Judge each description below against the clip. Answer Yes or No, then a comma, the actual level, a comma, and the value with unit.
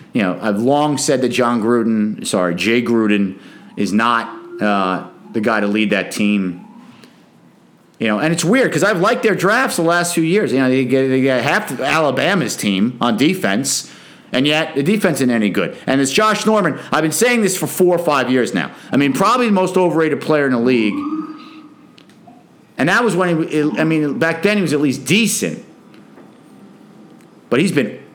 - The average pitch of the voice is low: No, medium, 145 Hz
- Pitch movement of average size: No, wide, 7.9 semitones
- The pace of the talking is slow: No, average, 200 wpm